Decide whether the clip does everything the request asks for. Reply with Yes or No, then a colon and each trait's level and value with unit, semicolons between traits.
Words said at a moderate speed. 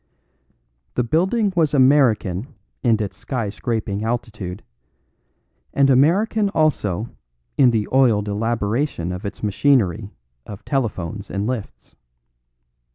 No: slow, 105 wpm